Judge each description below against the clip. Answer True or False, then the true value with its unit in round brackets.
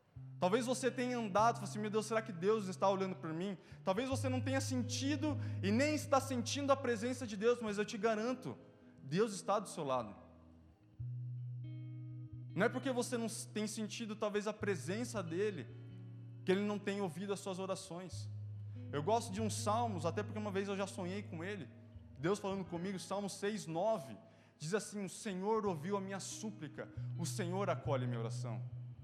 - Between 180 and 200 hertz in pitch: False (170 Hz)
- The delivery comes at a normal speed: False (190 wpm)